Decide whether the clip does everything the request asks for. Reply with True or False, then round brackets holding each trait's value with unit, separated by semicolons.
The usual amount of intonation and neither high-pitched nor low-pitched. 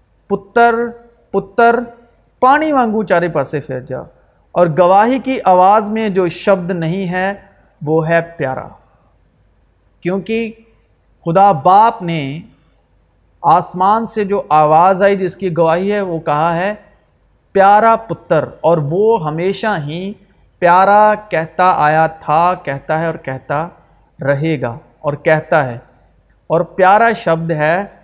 True (4.4 semitones; 180 Hz)